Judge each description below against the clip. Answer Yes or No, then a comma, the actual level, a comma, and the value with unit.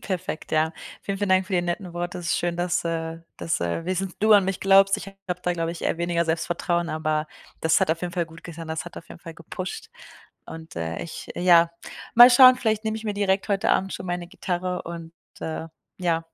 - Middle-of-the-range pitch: Yes, medium, 175 Hz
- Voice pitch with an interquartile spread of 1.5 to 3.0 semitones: Yes, average, 2.7 semitones